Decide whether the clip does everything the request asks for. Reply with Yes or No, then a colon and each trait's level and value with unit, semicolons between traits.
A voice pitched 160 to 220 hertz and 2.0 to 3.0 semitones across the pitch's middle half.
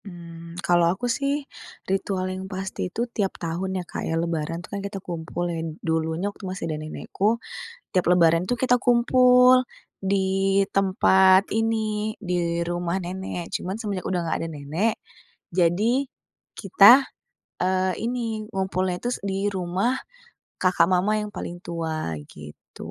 Yes: medium, 185 Hz; average, 2.7 semitones